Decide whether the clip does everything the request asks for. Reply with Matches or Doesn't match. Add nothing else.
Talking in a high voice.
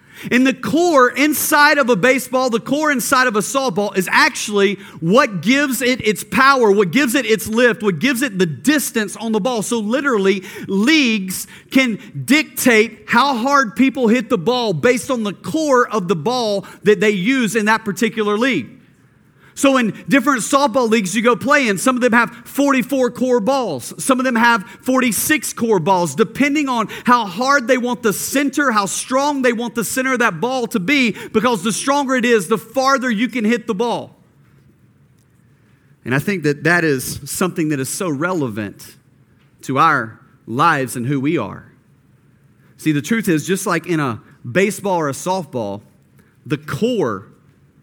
Matches